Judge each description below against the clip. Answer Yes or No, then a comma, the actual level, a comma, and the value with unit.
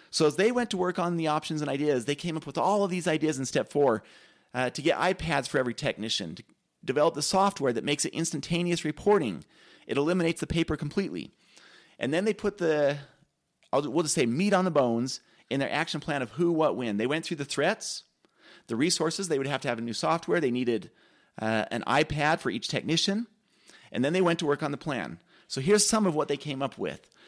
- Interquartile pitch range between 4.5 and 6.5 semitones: No, average, 3.8 semitones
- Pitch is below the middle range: No, medium, 155 Hz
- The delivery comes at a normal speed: No, fast, 230 wpm